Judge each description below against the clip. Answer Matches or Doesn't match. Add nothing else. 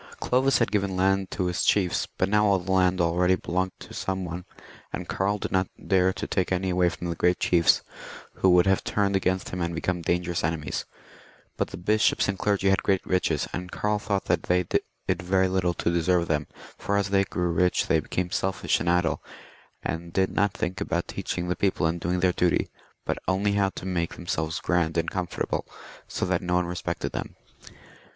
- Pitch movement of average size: Doesn't match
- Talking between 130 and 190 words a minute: Doesn't match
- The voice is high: Doesn't match